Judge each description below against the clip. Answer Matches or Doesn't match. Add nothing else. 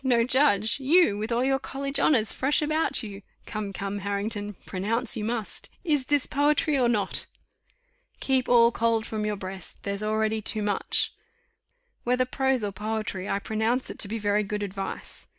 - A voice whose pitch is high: Matches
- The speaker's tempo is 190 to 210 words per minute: Doesn't match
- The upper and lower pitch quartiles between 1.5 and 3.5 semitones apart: Doesn't match